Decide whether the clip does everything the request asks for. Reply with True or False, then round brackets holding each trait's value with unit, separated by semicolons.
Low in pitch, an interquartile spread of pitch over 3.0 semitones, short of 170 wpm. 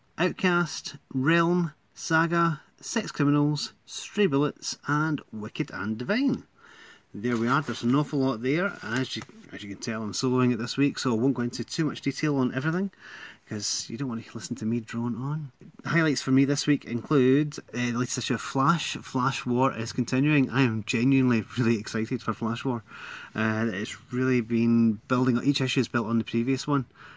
False (130 Hz; 3.6 semitones; 195 wpm)